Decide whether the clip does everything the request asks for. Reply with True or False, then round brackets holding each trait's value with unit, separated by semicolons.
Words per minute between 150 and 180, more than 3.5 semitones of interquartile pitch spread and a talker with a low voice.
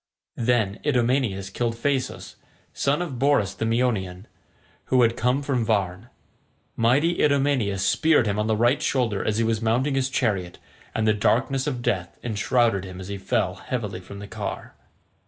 True (165 wpm; 4.4 semitones; 115 Hz)